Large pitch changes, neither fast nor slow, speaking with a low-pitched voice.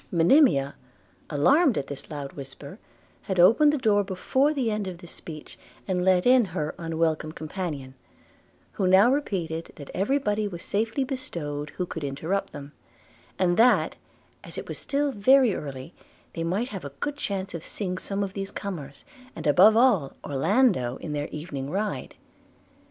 No: wide, 6.1 semitones; average, 165 wpm; medium, 185 Hz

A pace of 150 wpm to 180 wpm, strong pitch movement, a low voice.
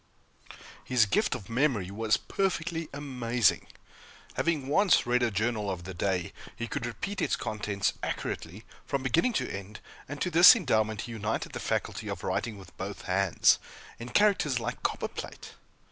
Yes: average, 160 wpm; wide, 5.9 semitones; low, 115 Hz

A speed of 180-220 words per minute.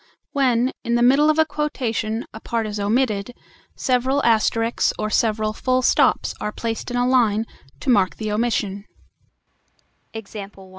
No: average, 145 wpm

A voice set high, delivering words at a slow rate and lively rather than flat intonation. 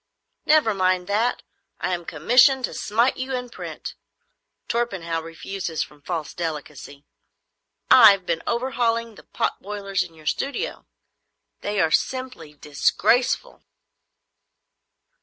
Yes: high, 195 Hz; slow, 115 wpm; wide, 6.6 semitones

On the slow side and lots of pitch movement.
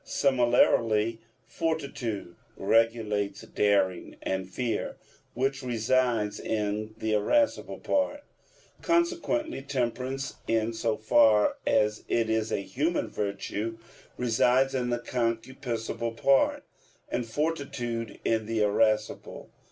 No: slow, 100 wpm; average, 3.4 semitones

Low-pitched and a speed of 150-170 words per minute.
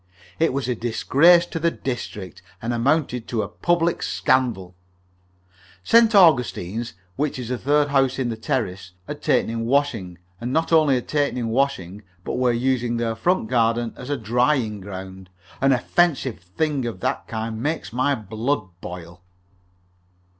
Yes: low, 125 Hz; average, 160 wpm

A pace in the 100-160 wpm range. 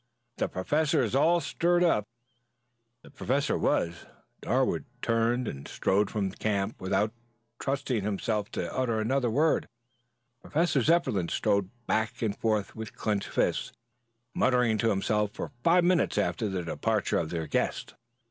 Yes: average, 145 wpm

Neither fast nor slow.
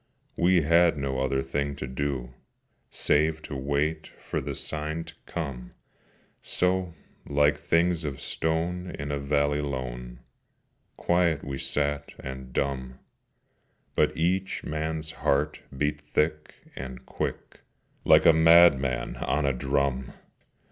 No: slow, 125 wpm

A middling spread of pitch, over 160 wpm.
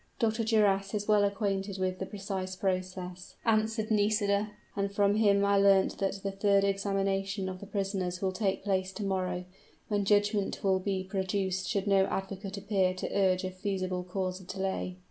No: narrow, 1.4 semitones; average, 175 wpm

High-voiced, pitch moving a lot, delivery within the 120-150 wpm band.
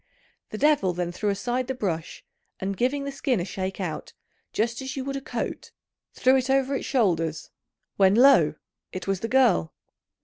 No: high, 225 Hz; wide, 6.1 semitones; average, 180 wpm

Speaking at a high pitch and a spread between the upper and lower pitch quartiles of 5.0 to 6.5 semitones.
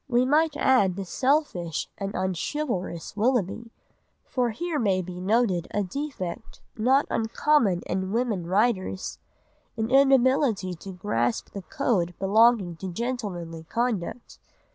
Yes: high, 215 Hz; wide, 5.5 semitones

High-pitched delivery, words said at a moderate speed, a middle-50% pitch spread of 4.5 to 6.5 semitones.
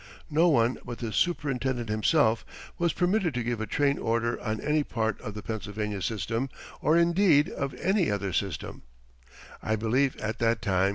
No: low, 120 Hz; average, 170 wpm; average, 5.3 semitones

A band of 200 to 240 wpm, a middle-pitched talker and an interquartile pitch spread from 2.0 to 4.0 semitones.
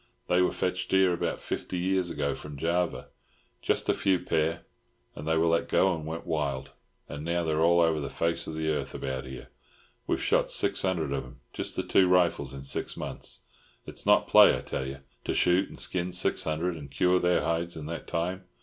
No: fast, 205 wpm; very low, 85 Hz; average, 2.9 semitones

